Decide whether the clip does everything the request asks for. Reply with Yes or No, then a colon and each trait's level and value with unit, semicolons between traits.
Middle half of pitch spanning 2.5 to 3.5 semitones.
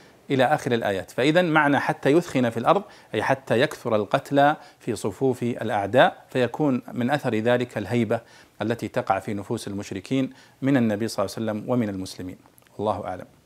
No: average, 3.9 semitones